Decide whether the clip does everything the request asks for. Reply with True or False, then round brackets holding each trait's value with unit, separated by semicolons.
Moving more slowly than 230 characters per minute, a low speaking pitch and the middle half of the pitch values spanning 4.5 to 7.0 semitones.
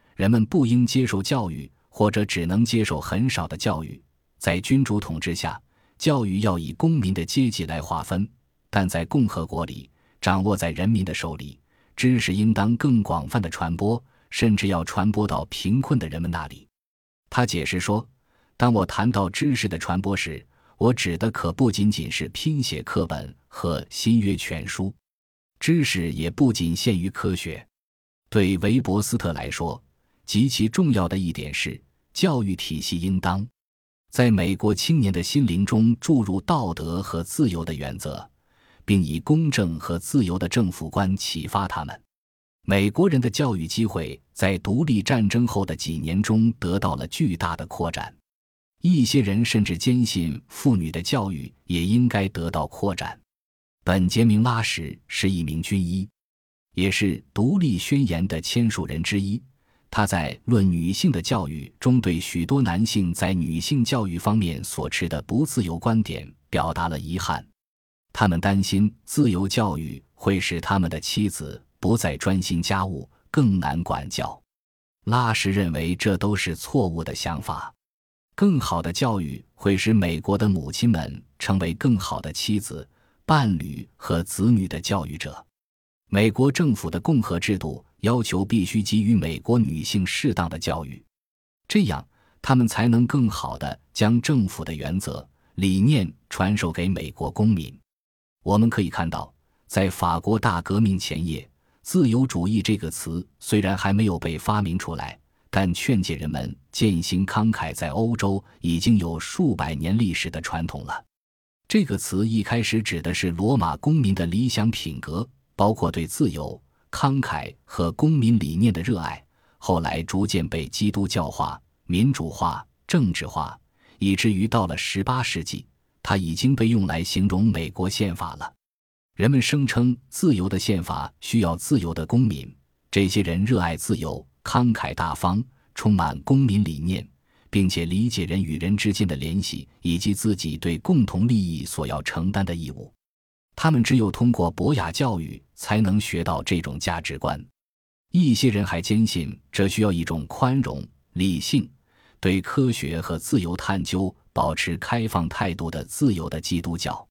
False (240 characters per minute; 100 Hz; 5.2 semitones)